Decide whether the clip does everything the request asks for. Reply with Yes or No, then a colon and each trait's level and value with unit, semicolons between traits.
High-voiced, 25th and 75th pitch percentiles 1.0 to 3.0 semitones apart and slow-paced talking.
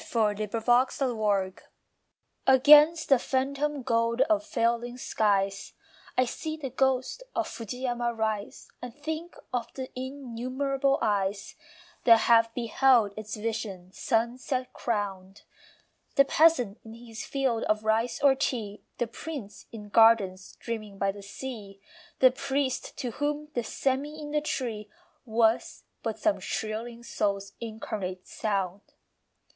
No: high, 235 Hz; average, 3.9 semitones; slow, 125 wpm